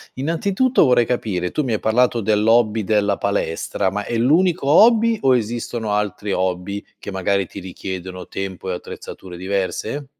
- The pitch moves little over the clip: No, average, 4.8 semitones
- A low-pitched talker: Yes, low, 105 Hz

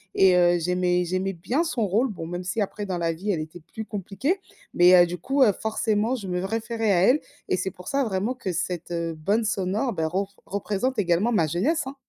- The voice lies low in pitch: No, high, 195 Hz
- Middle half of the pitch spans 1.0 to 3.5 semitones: No, average, 4.1 semitones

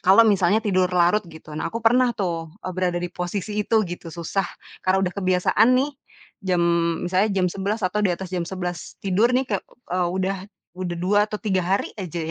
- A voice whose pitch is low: No, medium, 185 Hz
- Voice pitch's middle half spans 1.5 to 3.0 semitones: Yes, narrow, 2.6 semitones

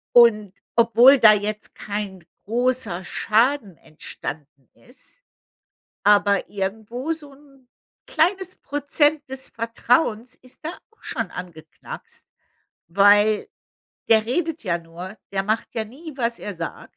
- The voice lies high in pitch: Yes, high, 225 Hz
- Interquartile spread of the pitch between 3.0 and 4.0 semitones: No, average, 4.7 semitones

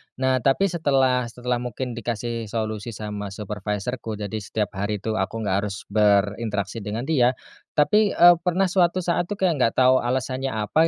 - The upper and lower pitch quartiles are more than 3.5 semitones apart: Yes, average, 4.3 semitones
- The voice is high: No, low, 120 Hz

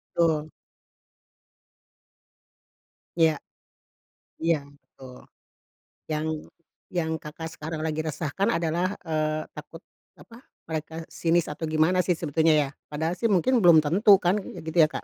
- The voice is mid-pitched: Yes, medium, 160 Hz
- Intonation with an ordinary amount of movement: No, narrow, 2.0 semitones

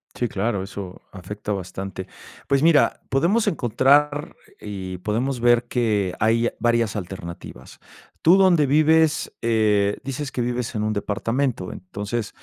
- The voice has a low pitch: Yes, low, 115 Hz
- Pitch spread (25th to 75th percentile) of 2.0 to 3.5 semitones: No, wide, 5.4 semitones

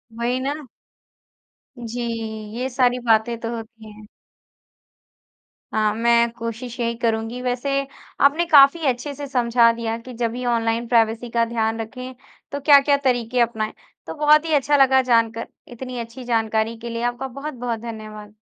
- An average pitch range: No, narrow, 2.2 semitones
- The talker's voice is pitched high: Yes, high, 235 Hz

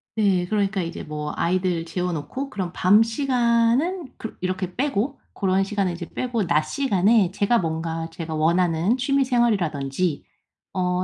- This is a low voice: No, medium, 185 Hz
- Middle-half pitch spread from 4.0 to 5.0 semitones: No, wide, 5.5 semitones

